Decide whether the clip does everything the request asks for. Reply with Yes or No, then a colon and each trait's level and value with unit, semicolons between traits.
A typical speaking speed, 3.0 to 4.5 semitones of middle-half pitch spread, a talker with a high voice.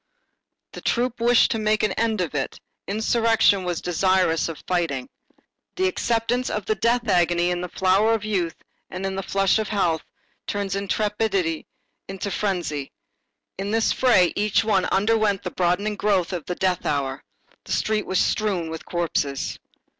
Yes: average, 160 wpm; average, 3.5 semitones; high, 195 Hz